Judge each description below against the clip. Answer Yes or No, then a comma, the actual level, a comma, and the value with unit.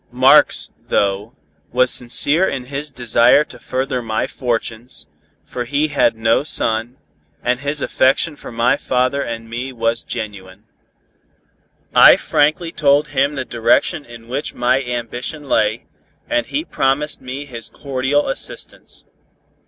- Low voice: Yes, low, 125 Hz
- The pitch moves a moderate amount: Yes, average, 3.4 semitones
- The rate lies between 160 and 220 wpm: No, slow, 135 wpm